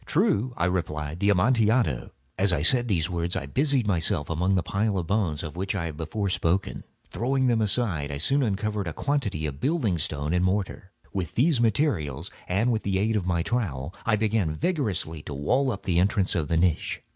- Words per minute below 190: No, fast, 205 wpm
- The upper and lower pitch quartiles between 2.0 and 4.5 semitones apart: No, wide, 5.4 semitones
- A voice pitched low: Yes, very low, 95 Hz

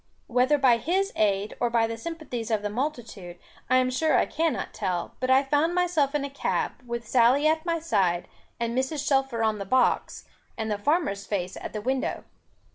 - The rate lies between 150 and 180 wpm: No, average, 200 wpm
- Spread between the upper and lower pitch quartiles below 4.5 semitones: No, average, 5.3 semitones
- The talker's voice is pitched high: Yes, very high, 255 Hz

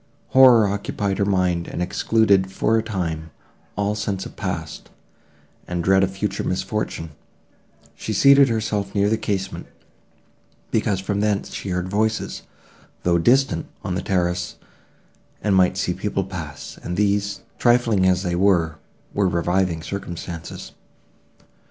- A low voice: Yes, very low, 95 Hz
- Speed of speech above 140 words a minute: No, slow, 135 wpm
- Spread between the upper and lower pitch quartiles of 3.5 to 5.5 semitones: No, average, 2.7 semitones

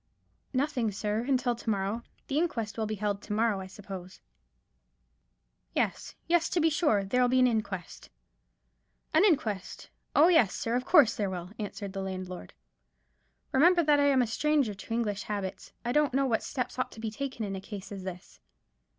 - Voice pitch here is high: Yes, high, 225 Hz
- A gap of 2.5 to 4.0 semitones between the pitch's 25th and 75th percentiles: No, average, 5.3 semitones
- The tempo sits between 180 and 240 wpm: Yes, average, 185 wpm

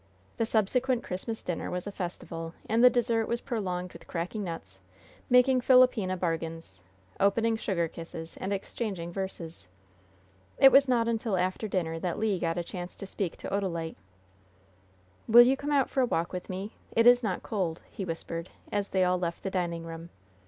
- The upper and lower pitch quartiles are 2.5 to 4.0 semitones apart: No, average, 5.1 semitones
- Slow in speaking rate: No, average, 180 wpm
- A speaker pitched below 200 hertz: Yes, high, 190 Hz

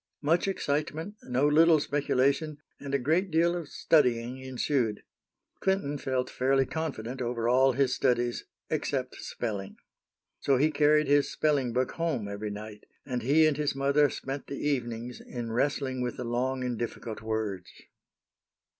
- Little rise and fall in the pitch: No, average, 3.5 semitones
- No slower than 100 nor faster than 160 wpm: Yes, average, 150 wpm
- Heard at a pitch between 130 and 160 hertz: Yes, low, 135 Hz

